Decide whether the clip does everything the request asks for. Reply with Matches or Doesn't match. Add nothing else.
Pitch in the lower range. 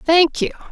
Doesn't match